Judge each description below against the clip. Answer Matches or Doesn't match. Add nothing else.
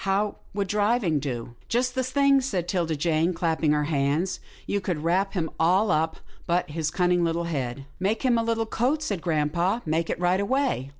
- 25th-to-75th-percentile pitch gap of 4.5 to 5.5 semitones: Matches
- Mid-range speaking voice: Matches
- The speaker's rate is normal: Doesn't match